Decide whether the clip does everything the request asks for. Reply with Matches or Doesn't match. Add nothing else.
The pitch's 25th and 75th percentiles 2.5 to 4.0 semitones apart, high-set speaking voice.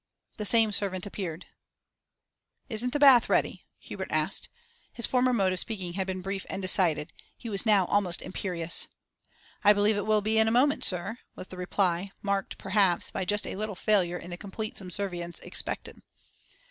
Matches